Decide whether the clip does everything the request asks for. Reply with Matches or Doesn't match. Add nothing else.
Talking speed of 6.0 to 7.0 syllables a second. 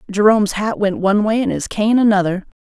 Matches